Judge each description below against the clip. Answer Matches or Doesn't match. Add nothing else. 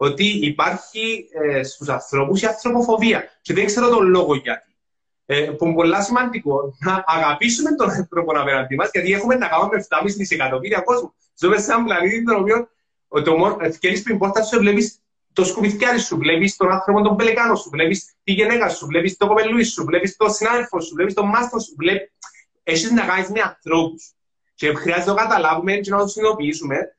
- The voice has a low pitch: Doesn't match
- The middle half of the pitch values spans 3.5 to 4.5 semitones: Doesn't match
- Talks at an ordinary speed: Doesn't match